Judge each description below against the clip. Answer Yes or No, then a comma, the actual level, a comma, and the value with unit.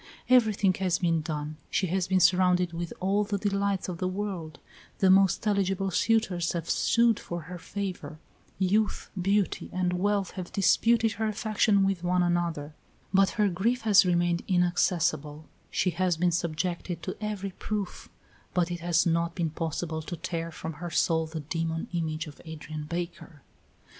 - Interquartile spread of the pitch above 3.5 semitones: No, average, 2.8 semitones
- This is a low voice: No, medium, 180 Hz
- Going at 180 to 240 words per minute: No, average, 165 wpm